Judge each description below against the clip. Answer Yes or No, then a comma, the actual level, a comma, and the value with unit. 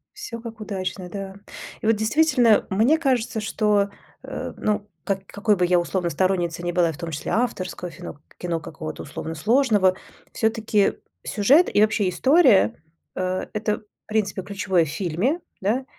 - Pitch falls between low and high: No, high, 200 Hz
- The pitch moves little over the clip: No, average, 3.8 semitones